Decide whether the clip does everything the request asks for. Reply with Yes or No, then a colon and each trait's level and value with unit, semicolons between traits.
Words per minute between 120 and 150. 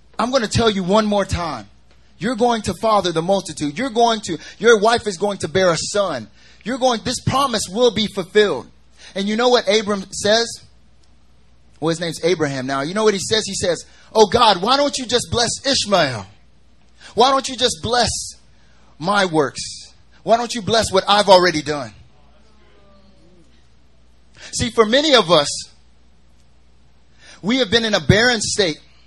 No: average, 175 wpm